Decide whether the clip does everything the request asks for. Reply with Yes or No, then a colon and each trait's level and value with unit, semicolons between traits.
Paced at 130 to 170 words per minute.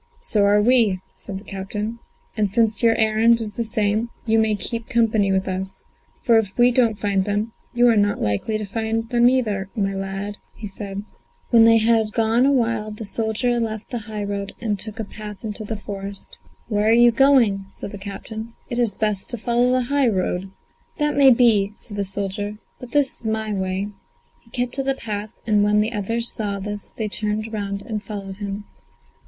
No: average, 200 wpm